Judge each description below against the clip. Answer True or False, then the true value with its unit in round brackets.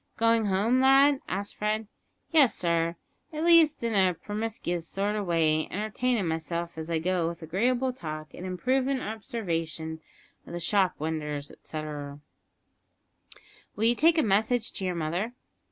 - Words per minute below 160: True (150 wpm)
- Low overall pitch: False (195 Hz)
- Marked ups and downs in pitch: True (6.0 semitones)